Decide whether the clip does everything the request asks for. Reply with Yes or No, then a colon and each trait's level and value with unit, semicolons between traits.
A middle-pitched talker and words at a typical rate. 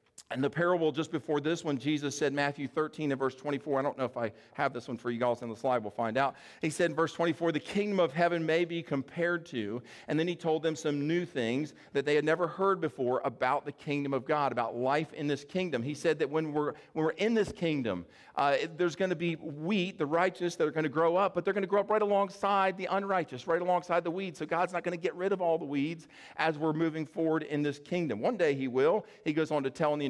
No: medium, 155 Hz; fast, 270 wpm